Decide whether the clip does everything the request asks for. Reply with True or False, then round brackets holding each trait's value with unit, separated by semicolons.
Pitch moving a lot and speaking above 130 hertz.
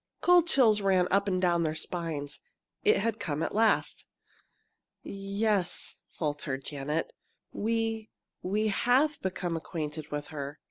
True (5.9 semitones; 185 Hz)